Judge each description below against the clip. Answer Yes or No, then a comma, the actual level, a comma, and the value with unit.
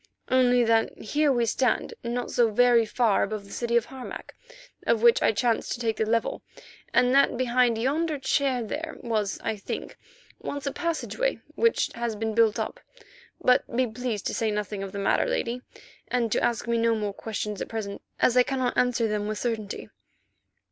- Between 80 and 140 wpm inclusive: No, average, 185 wpm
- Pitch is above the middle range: Yes, high, 235 Hz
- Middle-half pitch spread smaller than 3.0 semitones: Yes, narrow, 2.5 semitones